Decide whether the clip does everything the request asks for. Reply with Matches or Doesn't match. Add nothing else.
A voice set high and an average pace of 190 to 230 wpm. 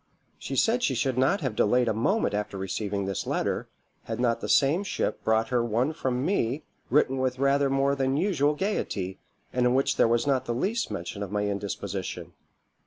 Doesn't match